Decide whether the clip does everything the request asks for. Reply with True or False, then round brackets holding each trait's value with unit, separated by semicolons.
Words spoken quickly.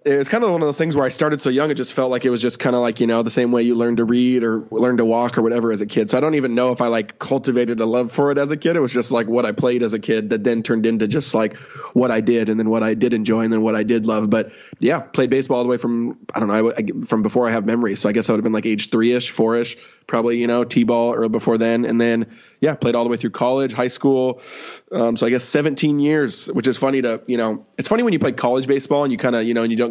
True (330 wpm)